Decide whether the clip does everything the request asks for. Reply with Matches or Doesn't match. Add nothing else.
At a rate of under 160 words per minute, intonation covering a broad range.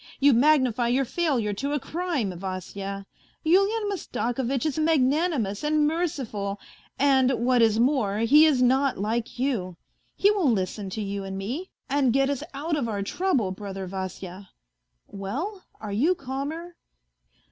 Matches